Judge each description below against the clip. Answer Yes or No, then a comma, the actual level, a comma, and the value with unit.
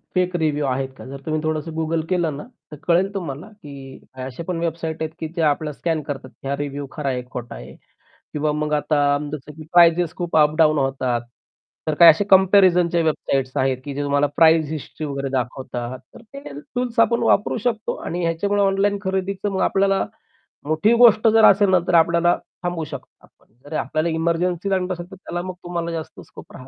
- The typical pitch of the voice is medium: Yes, medium, 160 Hz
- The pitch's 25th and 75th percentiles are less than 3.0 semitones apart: No, average, 4.0 semitones